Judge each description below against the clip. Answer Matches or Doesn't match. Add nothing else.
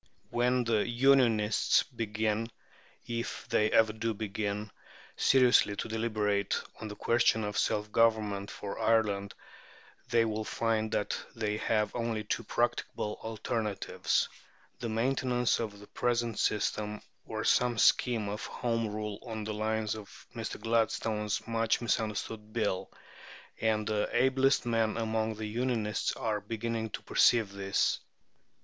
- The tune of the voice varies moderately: Doesn't match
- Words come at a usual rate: Doesn't match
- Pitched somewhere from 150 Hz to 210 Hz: Doesn't match